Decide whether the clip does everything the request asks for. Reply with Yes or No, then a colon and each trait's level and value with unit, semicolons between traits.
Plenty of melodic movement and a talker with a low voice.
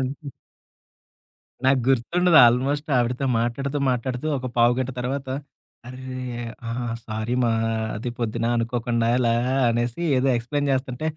No: narrow, 2.4 semitones; low, 125 Hz